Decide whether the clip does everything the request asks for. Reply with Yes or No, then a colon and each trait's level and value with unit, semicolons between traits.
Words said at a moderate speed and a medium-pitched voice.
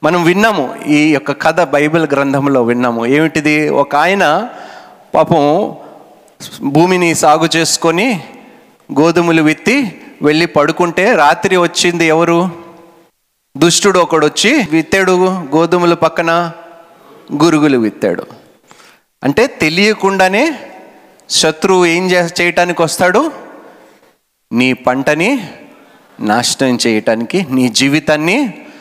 Yes: average, 90 wpm; medium, 165 Hz